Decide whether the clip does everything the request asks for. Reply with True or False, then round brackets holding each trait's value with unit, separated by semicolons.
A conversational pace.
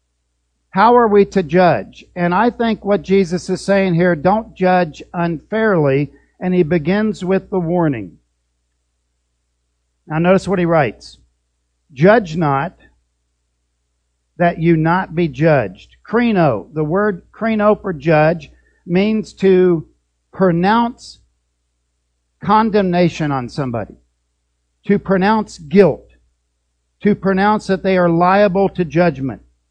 False (115 wpm)